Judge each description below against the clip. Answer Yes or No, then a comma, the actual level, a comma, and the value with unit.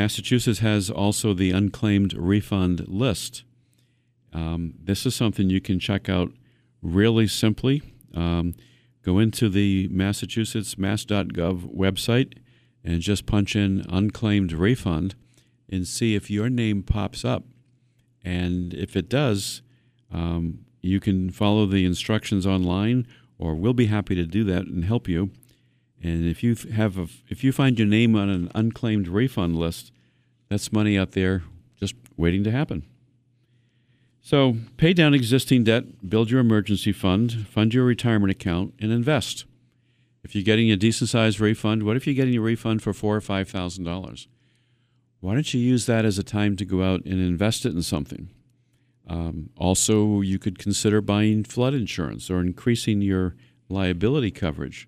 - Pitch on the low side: Yes, low, 105 Hz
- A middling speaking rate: Yes, average, 155 wpm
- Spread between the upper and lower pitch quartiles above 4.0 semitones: Yes, average, 4.5 semitones